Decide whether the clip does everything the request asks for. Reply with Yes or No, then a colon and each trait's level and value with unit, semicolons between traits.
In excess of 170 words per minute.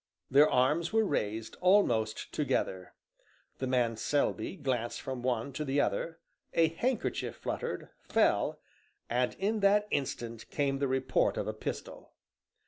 No: slow, 135 wpm